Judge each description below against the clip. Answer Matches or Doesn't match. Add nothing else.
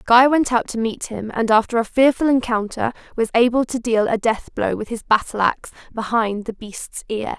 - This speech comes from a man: Doesn't match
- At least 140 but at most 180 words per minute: Doesn't match